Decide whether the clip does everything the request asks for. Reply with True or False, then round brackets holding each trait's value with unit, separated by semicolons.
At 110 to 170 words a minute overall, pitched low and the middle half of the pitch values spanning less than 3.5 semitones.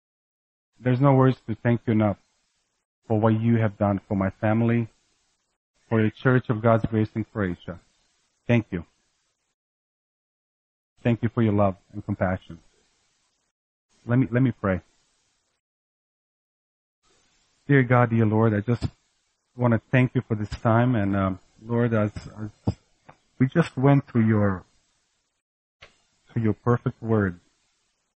True (135 wpm; 110 Hz; 3.0 semitones)